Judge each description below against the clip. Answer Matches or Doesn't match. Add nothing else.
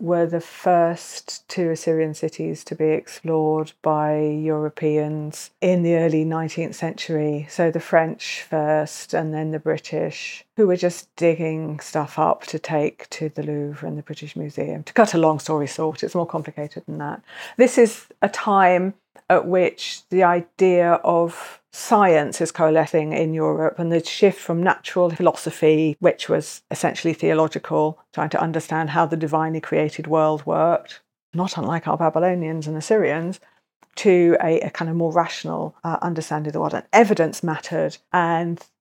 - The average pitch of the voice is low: Doesn't match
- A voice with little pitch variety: Matches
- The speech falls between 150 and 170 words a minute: Matches